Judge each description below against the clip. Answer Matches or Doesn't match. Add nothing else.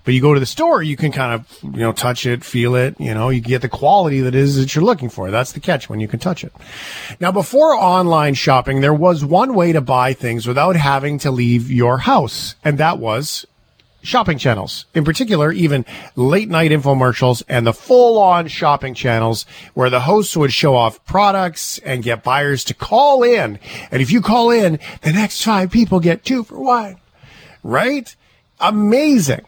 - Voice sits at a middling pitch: Matches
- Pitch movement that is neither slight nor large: Doesn't match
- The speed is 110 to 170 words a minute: Doesn't match